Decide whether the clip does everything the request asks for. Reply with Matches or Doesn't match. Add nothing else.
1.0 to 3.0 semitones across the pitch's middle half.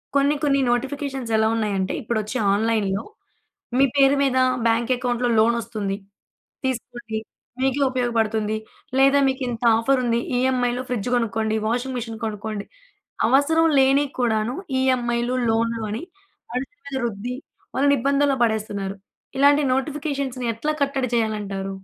Doesn't match